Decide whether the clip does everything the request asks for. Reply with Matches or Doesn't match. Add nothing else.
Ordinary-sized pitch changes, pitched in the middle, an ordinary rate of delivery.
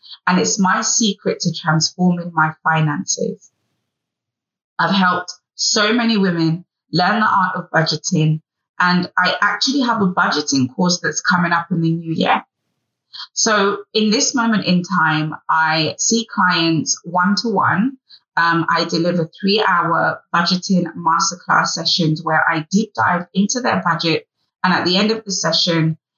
Matches